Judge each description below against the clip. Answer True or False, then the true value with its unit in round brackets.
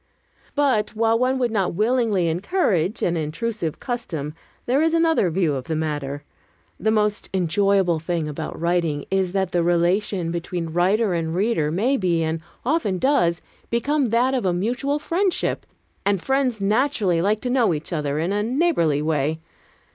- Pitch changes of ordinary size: False (6.2 semitones)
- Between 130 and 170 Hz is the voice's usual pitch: False (190 Hz)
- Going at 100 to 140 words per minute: False (160 wpm)